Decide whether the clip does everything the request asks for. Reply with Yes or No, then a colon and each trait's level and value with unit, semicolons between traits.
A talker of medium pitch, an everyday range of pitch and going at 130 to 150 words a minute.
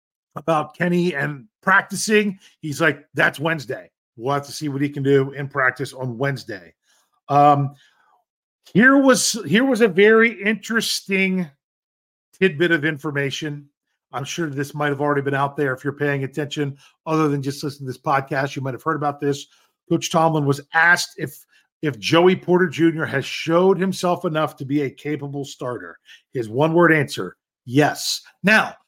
No: medium, 150 Hz; average, 3.7 semitones; average, 170 wpm